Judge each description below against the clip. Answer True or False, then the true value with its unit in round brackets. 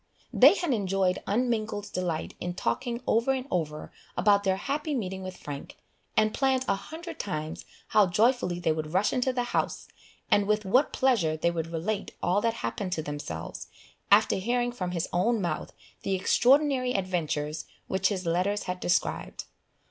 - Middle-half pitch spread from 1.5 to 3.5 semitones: False (5.6 semitones)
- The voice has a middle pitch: False (195 Hz)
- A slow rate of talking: False (165 wpm)